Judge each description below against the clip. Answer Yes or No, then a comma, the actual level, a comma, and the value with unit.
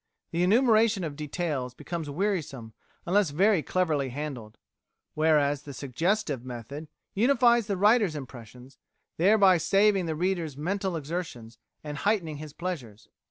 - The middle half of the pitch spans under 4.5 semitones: No, wide, 5.6 semitones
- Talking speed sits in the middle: No, slow, 125 wpm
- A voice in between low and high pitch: Yes, medium, 160 Hz